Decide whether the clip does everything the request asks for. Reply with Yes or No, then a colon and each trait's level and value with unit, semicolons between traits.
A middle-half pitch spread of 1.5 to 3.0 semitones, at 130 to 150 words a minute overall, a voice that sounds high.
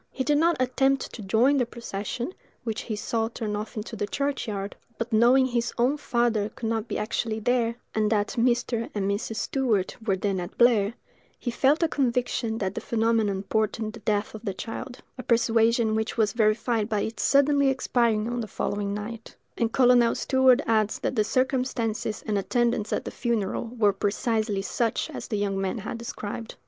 No: narrow, 2.5 semitones; average, 185 wpm; high, 225 Hz